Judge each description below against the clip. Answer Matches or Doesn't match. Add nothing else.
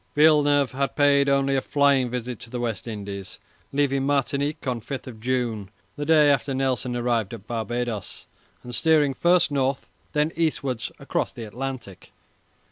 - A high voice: Doesn't match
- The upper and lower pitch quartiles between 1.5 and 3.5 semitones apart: Matches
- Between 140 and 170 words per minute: Matches